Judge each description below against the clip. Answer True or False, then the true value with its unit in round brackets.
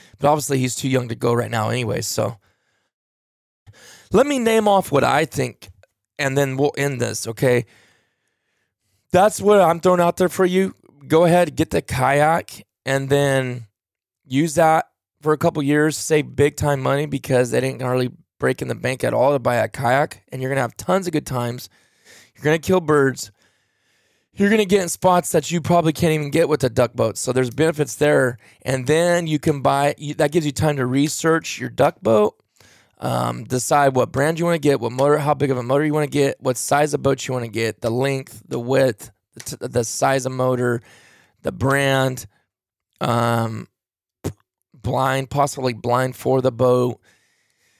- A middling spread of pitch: True (3.7 semitones)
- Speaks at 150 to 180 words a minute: False (190 wpm)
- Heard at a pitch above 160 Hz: False (135 Hz)